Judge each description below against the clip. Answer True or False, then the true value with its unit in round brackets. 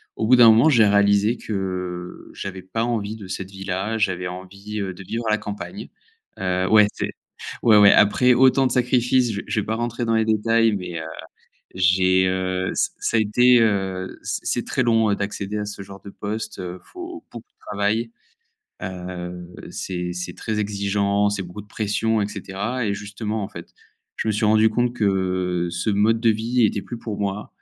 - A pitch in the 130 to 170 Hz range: False (105 Hz)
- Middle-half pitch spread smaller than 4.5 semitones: True (3.0 semitones)